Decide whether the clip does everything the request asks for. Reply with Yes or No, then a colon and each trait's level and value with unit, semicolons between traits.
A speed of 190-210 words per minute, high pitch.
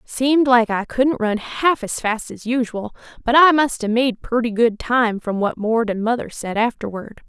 Yes: fast, 205 wpm; high, 235 Hz